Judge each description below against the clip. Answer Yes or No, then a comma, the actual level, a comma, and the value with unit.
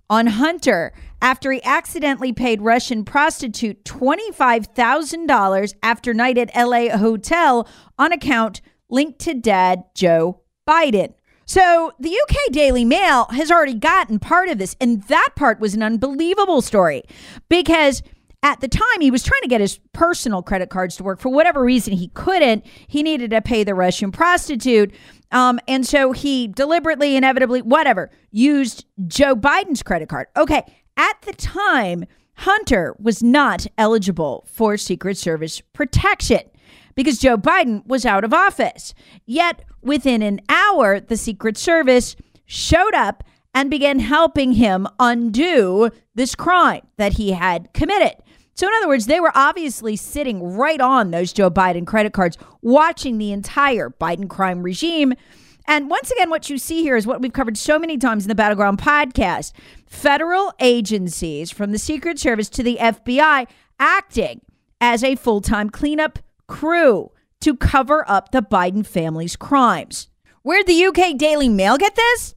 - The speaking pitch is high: Yes, very high, 255 Hz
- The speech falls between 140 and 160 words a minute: Yes, average, 155 wpm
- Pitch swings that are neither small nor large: No, wide, 6.1 semitones